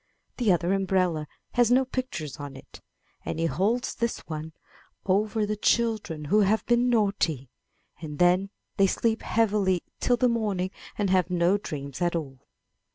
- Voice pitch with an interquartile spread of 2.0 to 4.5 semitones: No, average, 5.0 semitones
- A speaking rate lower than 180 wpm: Yes, average, 160 wpm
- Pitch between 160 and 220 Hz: Yes, high, 190 Hz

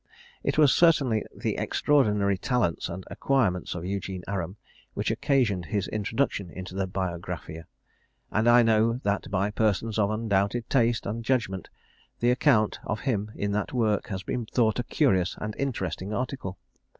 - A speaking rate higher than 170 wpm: No, average, 155 wpm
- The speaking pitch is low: Yes, low, 105 Hz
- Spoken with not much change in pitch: No, average, 4.0 semitones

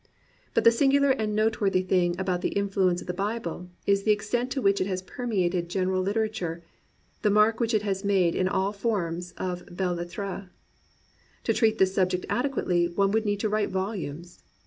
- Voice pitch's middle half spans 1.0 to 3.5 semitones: Yes, average, 3.0 semitones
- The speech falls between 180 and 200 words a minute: Yes, average, 190 wpm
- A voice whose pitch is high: Yes, high, 195 Hz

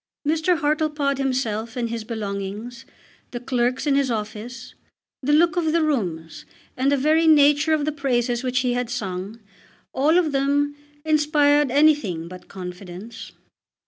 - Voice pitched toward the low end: No, very high, 260 Hz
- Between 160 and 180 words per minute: No, average, 145 wpm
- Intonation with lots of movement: No, average, 4.7 semitones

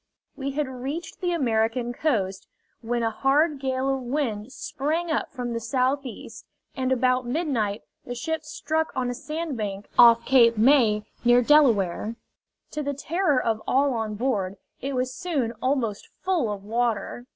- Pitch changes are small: No, average, 3.9 semitones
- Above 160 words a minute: No, average, 155 wpm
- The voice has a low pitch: No, very high, 255 Hz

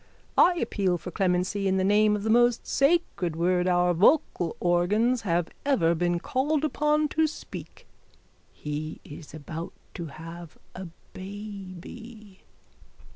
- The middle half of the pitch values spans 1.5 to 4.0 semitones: No, average, 5.1 semitones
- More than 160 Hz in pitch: Yes, high, 190 Hz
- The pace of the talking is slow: Yes, slow, 130 wpm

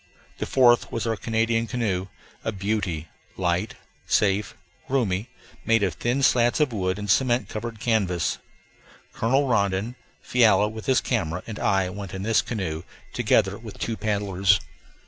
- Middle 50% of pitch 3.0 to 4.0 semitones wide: Yes, average, 3.5 semitones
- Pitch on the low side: Yes, low, 105 Hz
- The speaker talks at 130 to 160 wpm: Yes, average, 145 wpm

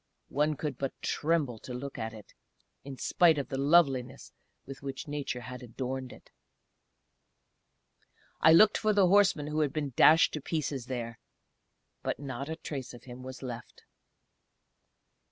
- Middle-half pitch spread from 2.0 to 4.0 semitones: Yes, average, 3.4 semitones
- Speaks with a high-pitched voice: No, medium, 140 Hz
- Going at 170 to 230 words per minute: No, average, 155 wpm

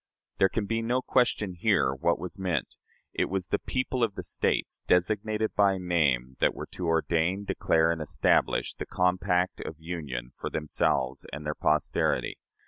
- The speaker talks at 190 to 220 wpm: No, average, 165 wpm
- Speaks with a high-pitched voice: No, very low, 90 Hz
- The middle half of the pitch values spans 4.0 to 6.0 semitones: Yes, average, 4.4 semitones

